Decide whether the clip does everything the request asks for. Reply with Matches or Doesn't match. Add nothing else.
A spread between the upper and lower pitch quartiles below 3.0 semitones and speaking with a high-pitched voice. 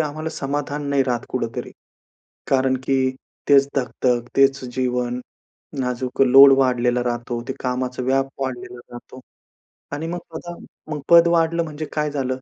Doesn't match